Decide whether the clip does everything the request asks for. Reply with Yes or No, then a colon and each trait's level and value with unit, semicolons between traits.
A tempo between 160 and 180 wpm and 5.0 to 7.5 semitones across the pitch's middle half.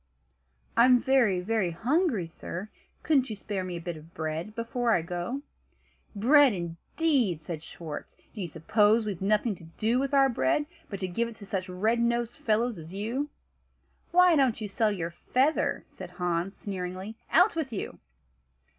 Yes: average, 170 wpm; wide, 5.5 semitones